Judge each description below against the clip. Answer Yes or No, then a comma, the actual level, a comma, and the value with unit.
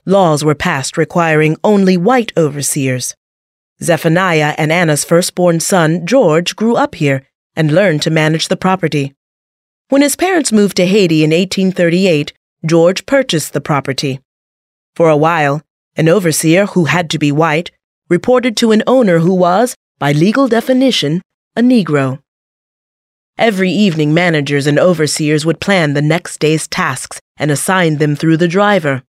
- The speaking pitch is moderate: Yes, medium, 165 Hz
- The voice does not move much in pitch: No, average, 4.1 semitones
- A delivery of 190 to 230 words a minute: No, average, 150 wpm